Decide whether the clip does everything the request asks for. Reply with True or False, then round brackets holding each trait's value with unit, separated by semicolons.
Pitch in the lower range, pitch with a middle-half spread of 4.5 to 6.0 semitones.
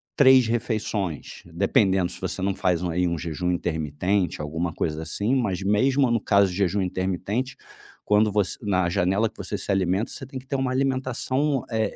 True (100 Hz; 4.8 semitones)